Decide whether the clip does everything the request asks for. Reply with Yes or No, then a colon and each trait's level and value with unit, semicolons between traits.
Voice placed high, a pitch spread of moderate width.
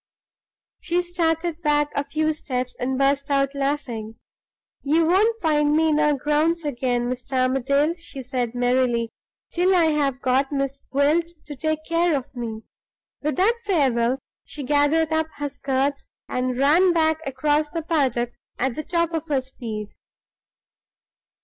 Yes: very high, 290 Hz; average, 3.6 semitones